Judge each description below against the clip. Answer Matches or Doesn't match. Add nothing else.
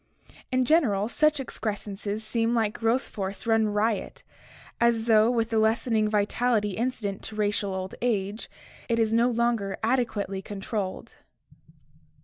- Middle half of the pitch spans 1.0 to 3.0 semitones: Matches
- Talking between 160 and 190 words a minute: Doesn't match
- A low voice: Doesn't match